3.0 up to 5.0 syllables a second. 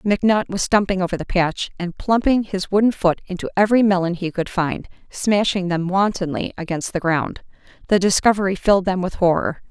No: 5.5 syllables/s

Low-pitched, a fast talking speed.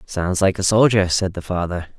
Yes: very low, 95 Hz; fast, 210 wpm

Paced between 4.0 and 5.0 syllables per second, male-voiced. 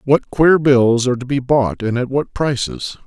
Yes: 4.5 syllables/s; male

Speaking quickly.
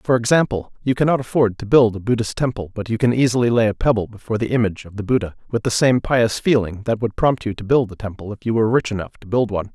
Yes: fast, 265 wpm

